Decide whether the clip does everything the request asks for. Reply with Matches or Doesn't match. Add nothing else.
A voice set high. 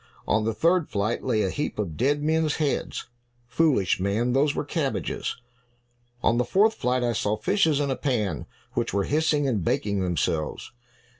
Doesn't match